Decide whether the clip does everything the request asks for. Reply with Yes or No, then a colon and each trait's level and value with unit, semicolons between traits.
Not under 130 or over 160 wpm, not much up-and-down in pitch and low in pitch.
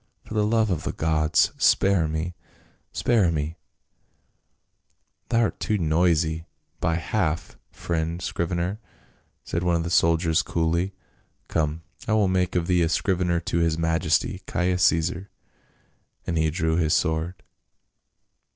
Yes: average, 140 wpm; narrow, 2.1 semitones; very low, 85 Hz